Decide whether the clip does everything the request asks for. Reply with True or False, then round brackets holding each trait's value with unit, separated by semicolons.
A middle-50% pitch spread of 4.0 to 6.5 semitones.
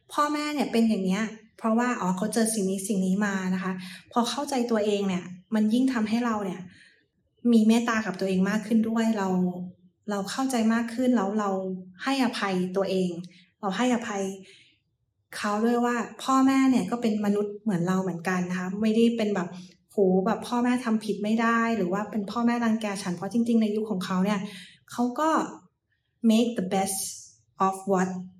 False (3.6 semitones)